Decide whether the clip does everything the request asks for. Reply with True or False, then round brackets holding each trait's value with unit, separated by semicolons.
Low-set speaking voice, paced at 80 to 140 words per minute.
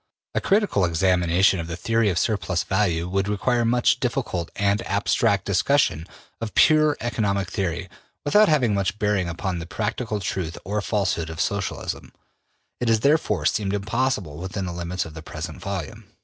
False (100 Hz; 165 wpm)